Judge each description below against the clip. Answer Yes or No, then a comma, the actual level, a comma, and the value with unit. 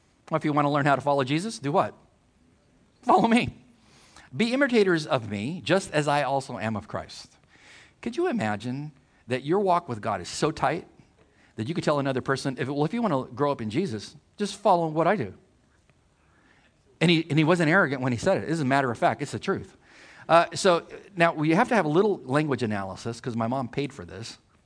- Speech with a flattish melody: No, average, 4.8 semitones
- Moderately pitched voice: Yes, medium, 145 Hz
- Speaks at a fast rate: Yes, fast, 225 wpm